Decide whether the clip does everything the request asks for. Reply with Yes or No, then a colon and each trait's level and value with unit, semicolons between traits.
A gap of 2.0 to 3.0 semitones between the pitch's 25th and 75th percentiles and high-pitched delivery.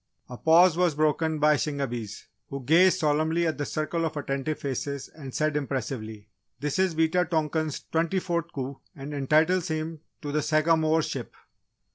No: narrow, 2.6 semitones; medium, 155 Hz